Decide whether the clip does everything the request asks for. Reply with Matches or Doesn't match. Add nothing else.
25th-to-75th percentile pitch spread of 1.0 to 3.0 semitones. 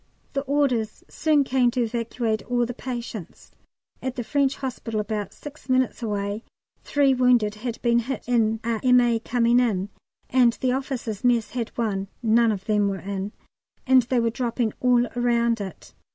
Matches